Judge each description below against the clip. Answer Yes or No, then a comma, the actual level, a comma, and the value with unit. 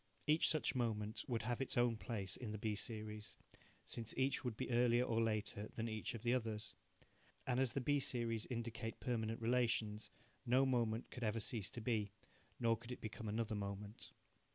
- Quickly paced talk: No, average, 185 wpm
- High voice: No, low, 115 Hz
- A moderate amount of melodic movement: No, narrow, 2.3 semitones